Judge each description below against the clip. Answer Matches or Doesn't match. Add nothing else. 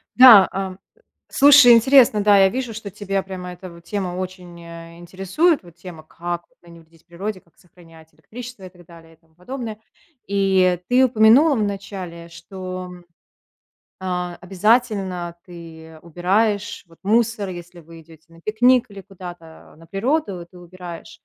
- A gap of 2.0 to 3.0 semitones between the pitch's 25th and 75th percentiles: Doesn't match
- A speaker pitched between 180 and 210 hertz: Matches